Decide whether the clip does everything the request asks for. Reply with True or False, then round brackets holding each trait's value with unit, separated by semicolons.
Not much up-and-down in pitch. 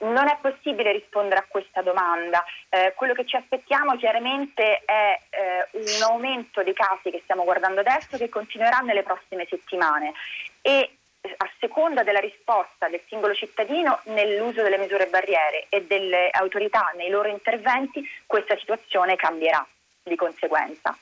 False (4.1 semitones)